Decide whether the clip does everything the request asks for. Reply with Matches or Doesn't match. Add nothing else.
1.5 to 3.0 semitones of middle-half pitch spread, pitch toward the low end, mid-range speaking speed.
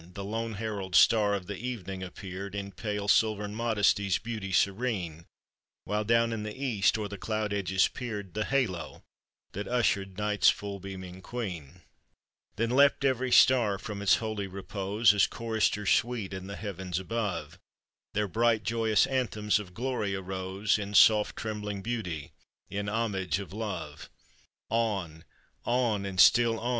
Matches